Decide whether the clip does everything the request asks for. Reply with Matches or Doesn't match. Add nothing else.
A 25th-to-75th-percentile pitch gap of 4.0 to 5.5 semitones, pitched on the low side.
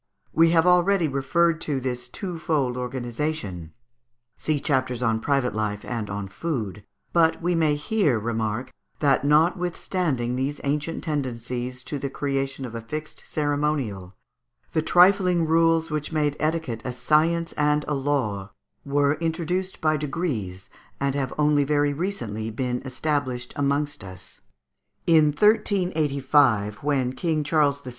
Doesn't match